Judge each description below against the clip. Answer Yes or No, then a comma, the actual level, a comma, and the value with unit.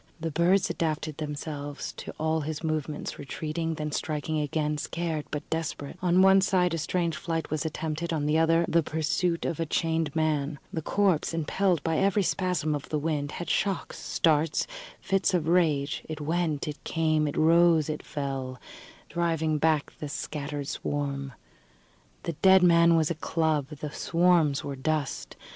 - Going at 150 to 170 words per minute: Yes, average, 165 wpm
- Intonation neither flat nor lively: No, narrow, 2.2 semitones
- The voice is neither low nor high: Yes, medium, 160 Hz